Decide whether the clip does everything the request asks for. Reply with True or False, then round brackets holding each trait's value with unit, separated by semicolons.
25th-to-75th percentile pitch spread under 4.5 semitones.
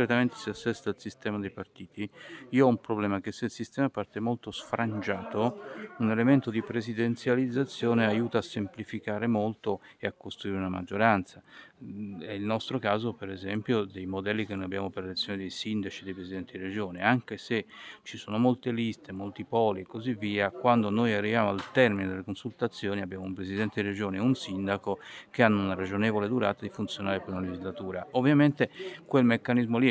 True (3.1 semitones)